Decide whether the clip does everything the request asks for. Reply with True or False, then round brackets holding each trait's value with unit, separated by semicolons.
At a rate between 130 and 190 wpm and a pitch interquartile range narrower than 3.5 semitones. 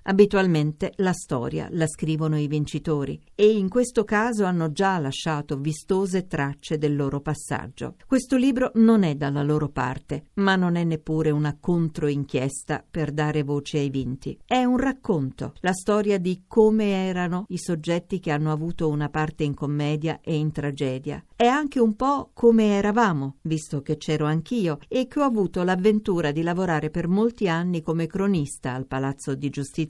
False (165 wpm; 4.9 semitones)